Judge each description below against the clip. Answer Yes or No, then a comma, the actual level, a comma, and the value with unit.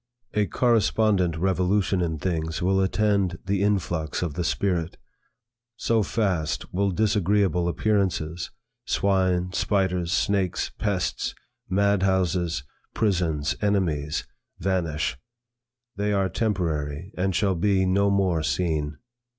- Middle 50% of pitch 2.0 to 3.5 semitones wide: Yes, average, 3.0 semitones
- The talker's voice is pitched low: Yes, very low, 95 Hz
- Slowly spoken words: Yes, slow, 105 wpm